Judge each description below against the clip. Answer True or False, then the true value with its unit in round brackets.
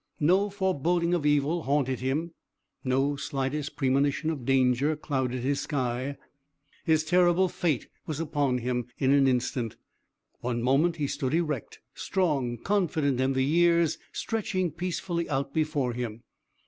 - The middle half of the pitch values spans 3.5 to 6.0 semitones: True (4.2 semitones)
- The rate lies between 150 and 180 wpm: False (135 wpm)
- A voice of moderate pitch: True (145 Hz)